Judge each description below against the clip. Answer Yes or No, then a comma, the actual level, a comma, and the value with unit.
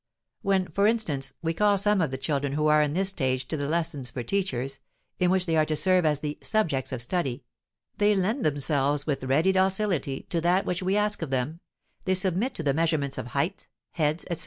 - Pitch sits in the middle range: Yes, medium, 160 Hz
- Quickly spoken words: Yes, fast, 215 wpm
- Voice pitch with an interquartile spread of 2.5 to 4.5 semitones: No, average, 5.2 semitones